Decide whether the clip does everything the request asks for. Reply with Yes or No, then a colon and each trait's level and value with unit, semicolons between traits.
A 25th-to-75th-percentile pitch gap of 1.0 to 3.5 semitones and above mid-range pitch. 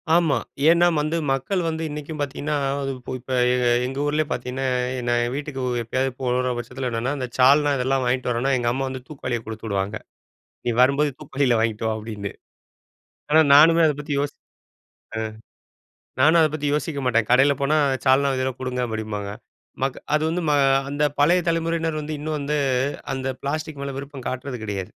No: average, 3.2 semitones; low, 135 Hz